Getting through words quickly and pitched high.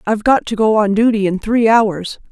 Yes: fast, 235 wpm; high, 215 Hz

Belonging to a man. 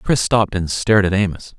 Yes: male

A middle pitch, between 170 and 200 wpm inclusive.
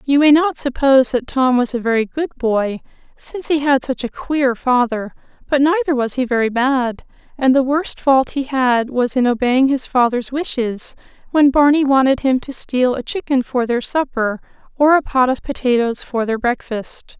No: very high, 260 Hz; average, 190 wpm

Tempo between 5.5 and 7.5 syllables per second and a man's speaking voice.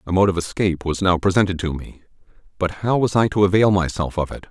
Yes: 6.3 syllables/s; male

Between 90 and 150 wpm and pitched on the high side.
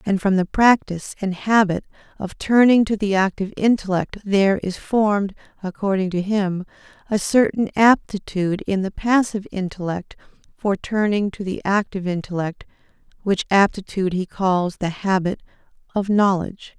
Yes: average, 140 wpm; high, 195 Hz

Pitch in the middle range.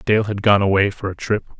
No: low, 100 Hz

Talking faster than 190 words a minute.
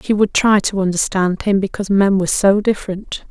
Yes: average, 200 wpm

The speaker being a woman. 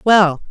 Yes: female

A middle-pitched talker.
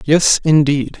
Yes: medium, 150 Hz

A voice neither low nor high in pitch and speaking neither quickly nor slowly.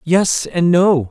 Yes: medium, 170 Hz; average, 165 wpm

